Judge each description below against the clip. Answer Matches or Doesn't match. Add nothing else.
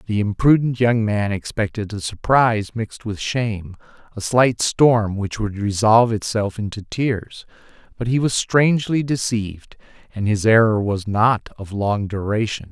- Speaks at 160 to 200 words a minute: Doesn't match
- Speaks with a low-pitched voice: Matches